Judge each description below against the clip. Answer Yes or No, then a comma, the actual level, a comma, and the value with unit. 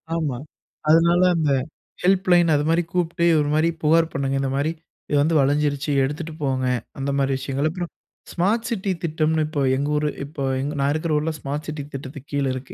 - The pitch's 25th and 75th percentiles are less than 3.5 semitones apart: Yes, average, 2.9 semitones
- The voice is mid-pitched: Yes, medium, 150 Hz